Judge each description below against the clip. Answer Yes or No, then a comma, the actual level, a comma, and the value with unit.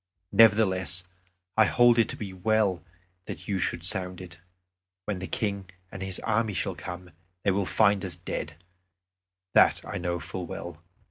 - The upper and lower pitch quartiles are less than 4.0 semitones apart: Yes, average, 2.8 semitones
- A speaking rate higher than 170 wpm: No, average, 160 wpm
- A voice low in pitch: Yes, very low, 95 Hz